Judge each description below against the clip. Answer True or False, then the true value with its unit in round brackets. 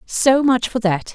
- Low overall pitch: False (235 Hz)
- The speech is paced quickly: True (210 wpm)